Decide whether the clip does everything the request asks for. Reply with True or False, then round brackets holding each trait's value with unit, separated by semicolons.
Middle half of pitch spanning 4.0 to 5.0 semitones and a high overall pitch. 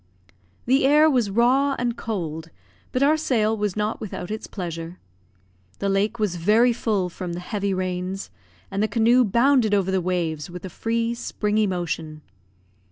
True (4.6 semitones; 210 Hz)